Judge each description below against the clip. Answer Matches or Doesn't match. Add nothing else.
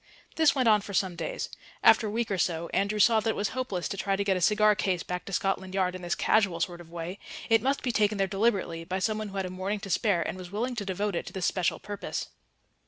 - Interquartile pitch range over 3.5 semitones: Doesn't match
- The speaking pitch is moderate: Doesn't match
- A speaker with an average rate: Doesn't match